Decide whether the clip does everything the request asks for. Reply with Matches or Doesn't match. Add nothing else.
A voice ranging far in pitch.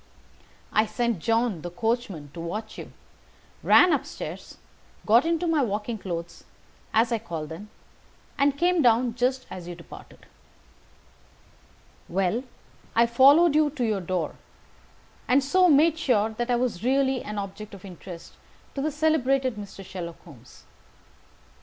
Matches